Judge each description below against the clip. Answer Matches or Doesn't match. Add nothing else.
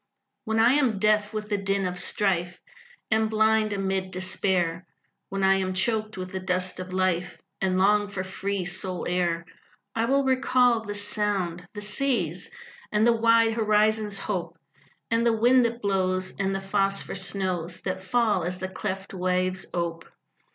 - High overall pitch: Matches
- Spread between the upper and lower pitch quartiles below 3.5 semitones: Matches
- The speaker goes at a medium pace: Matches